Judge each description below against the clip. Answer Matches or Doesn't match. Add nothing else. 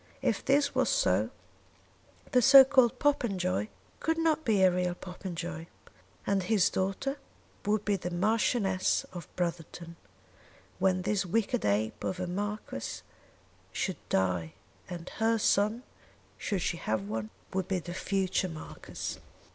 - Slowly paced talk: Matches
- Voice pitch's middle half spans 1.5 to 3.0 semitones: Doesn't match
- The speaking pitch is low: Doesn't match